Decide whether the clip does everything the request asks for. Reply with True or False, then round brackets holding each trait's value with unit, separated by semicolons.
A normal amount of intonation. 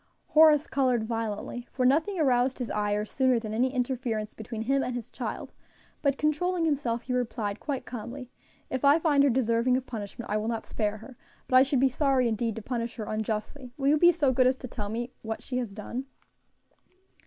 True (3.3 semitones)